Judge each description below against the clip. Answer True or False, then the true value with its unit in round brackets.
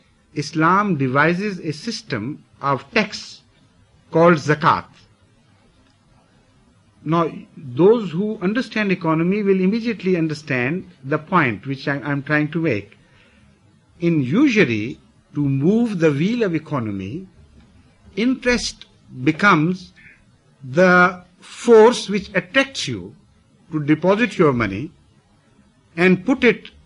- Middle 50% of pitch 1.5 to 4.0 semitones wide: False (5.6 semitones)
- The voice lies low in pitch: False (175 Hz)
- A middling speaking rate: False (105 wpm)